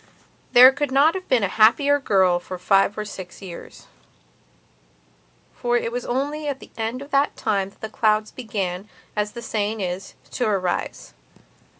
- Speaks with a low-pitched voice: No, high, 220 Hz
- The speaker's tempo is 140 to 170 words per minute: Yes, average, 165 wpm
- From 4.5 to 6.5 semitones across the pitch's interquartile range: Yes, average, 4.9 semitones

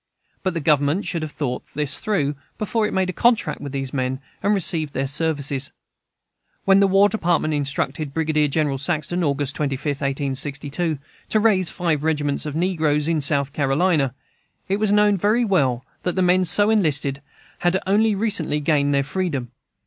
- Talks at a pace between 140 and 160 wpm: No, average, 170 wpm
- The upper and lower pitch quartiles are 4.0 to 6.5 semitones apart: Yes, average, 4.9 semitones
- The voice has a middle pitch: Yes, medium, 155 Hz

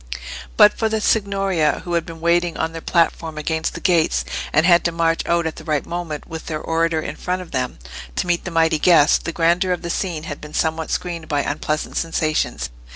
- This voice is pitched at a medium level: Yes, medium, 165 Hz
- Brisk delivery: Yes, fast, 220 wpm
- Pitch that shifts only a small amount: Yes, narrow, 1.7 semitones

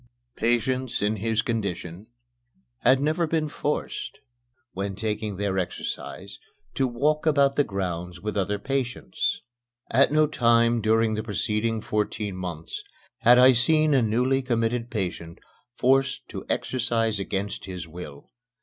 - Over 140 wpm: No, slow, 135 wpm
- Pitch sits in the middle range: No, low, 115 Hz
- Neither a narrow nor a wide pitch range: Yes, average, 4.6 semitones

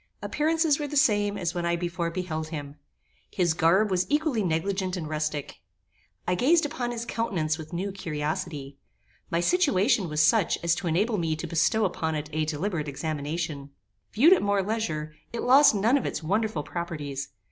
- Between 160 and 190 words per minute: Yes, average, 175 wpm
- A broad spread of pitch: Yes, wide, 5.7 semitones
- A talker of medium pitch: Yes, medium, 175 Hz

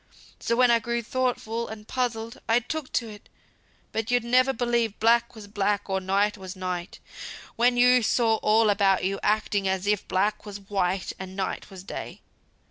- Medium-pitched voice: No, high, 215 Hz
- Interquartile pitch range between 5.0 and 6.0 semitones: No, average, 3.3 semitones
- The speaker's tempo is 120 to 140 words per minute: No, average, 180 wpm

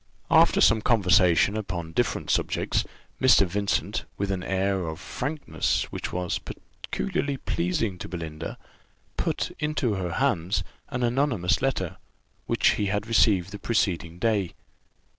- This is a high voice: No, low, 100 Hz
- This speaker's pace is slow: Yes, slow, 130 wpm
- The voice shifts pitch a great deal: No, average, 4.8 semitones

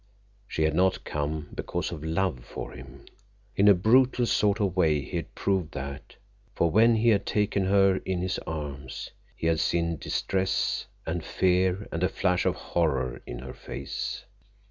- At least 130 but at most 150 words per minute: No, average, 170 wpm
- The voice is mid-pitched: No, very low, 90 Hz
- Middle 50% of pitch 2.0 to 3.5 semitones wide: No, average, 3.9 semitones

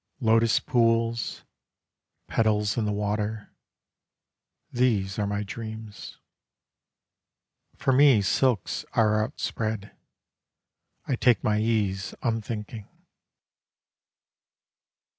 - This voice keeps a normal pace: No, slow, 80 wpm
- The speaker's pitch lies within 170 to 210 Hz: No, low, 110 Hz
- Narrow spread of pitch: Yes, narrow, 1.8 semitones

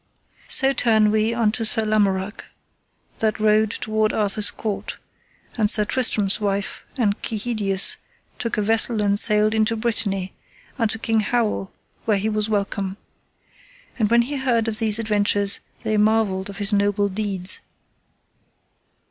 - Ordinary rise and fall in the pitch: No, narrow, 1.7 semitones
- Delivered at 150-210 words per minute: No, average, 140 wpm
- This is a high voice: Yes, high, 215 Hz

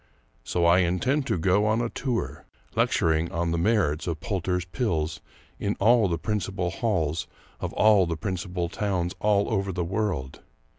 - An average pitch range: Yes, average, 3.8 semitones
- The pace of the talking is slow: No, average, 160 wpm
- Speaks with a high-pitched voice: No, very low, 90 Hz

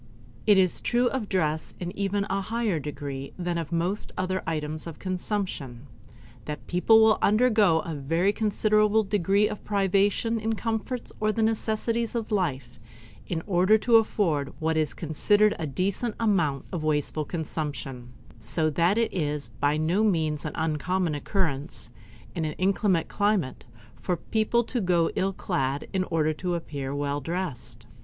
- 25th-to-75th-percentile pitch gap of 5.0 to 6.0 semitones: Yes, wide, 5.5 semitones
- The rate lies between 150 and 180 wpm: Yes, average, 160 wpm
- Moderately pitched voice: Yes, medium, 180 Hz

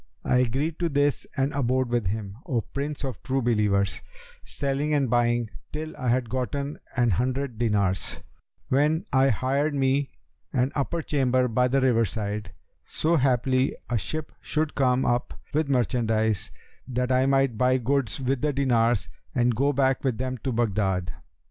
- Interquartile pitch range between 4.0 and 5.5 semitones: No, average, 2.9 semitones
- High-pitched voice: No, low, 130 Hz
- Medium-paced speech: Yes, average, 160 wpm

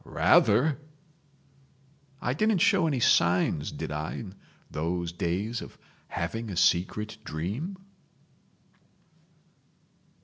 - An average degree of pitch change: No, wide, 8.1 semitones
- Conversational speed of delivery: No, slow, 95 wpm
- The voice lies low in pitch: Yes, low, 105 Hz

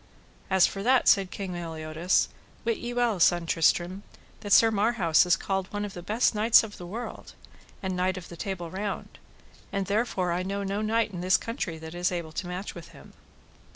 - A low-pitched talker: No, high, 190 Hz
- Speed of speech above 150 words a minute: Yes, average, 200 wpm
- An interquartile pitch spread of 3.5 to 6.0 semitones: No, average, 3.1 semitones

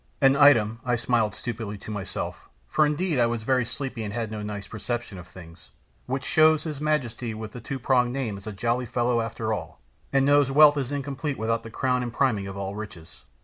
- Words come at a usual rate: No, fast, 215 wpm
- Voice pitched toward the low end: Yes, low, 120 Hz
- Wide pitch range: No, average, 4.0 semitones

